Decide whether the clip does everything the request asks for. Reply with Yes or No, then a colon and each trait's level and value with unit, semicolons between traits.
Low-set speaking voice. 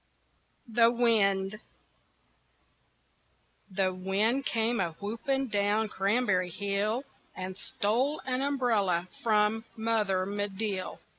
No: high, 210 Hz